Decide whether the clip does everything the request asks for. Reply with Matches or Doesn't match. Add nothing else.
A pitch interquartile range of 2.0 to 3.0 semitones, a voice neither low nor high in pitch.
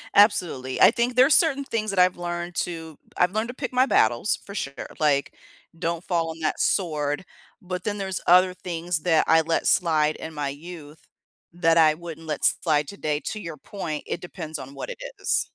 Doesn't match